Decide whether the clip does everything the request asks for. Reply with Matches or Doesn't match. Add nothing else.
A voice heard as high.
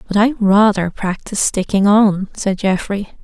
Matches